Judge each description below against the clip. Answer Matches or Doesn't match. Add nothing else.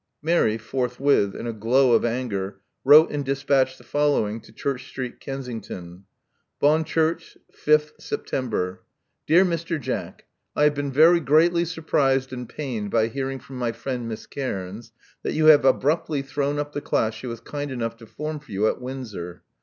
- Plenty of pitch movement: Doesn't match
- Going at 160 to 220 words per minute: Matches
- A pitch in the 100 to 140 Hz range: Matches